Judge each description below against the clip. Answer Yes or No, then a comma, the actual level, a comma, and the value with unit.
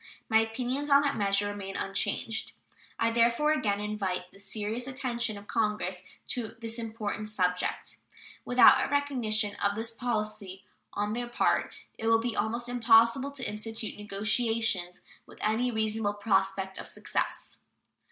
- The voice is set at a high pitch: Yes, high, 220 Hz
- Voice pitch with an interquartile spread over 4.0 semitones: No, average, 2.7 semitones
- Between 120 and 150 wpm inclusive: Yes, average, 140 wpm